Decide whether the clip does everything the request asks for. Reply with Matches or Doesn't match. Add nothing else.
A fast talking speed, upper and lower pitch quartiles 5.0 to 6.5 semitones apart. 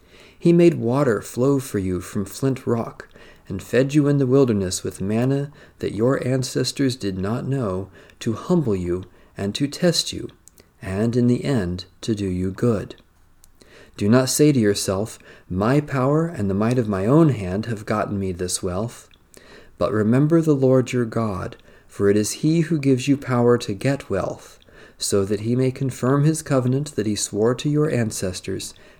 Doesn't match